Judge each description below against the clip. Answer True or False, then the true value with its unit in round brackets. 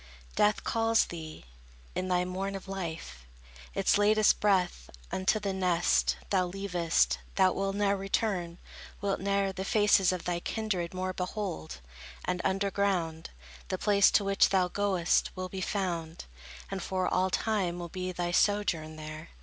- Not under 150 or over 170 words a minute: True (155 wpm)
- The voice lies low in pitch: False (185 Hz)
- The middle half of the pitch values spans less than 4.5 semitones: True (2.4 semitones)